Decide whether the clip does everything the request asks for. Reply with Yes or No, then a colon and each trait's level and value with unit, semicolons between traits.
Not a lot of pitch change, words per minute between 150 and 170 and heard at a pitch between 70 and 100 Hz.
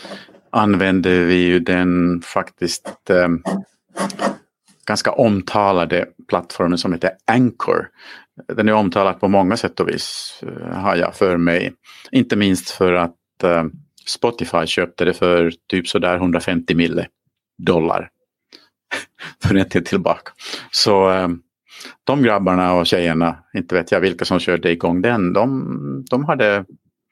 No: narrow, 2.0 semitones; average, 130 wpm; very low, 90 Hz